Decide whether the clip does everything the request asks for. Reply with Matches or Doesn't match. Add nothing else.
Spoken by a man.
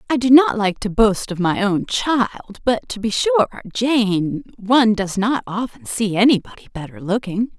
Doesn't match